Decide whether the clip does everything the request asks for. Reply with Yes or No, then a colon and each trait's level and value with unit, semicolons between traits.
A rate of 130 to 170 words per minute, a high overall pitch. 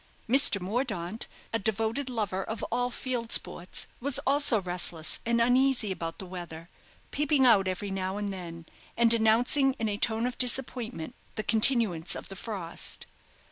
Yes: average, 155 wpm; high, 220 Hz